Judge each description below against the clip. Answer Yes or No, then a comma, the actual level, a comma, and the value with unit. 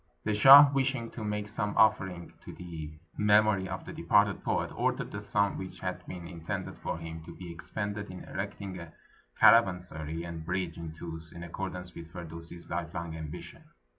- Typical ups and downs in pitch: Yes, average, 3.7 semitones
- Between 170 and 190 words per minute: Yes, average, 180 wpm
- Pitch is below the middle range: Yes, very low, 90 Hz